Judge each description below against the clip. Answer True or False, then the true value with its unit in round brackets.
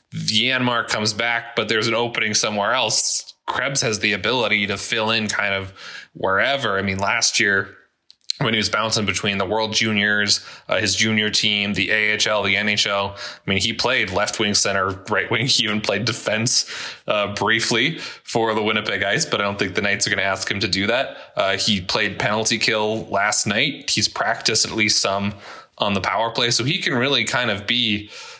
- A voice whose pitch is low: True (105 Hz)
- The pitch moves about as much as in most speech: False (1.9 semitones)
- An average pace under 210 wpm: True (200 wpm)